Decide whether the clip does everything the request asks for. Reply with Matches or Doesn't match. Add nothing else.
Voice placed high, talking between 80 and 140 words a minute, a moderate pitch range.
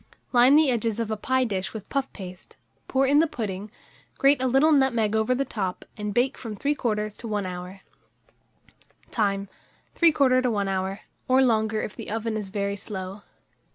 Doesn't match